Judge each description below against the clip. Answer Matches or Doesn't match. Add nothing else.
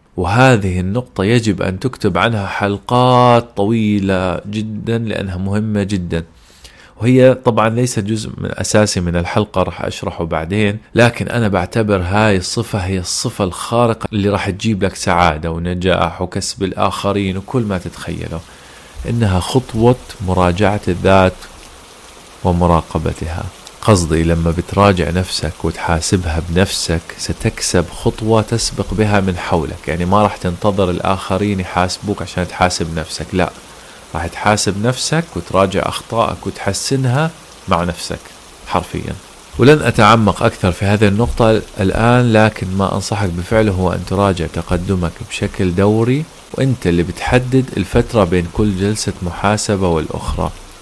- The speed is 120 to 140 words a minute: Matches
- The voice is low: Matches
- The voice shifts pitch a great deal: Doesn't match